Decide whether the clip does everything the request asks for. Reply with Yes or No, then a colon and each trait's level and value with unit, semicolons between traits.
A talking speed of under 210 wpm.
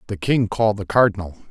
Yes: average, 200 wpm